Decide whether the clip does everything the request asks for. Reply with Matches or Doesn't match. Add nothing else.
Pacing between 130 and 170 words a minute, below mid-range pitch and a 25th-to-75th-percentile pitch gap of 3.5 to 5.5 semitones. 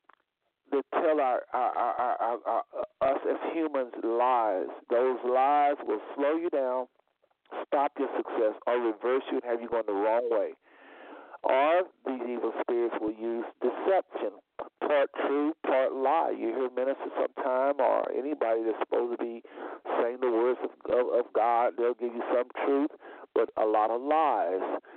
Matches